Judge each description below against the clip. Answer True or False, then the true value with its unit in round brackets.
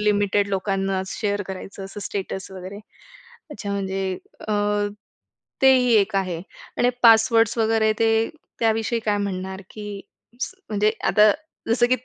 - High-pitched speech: True (205 Hz)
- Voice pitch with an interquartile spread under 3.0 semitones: True (2.5 semitones)